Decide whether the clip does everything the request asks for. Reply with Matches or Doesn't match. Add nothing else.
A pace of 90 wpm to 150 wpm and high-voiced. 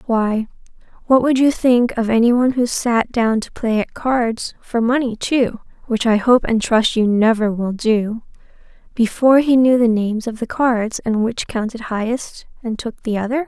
Doesn't match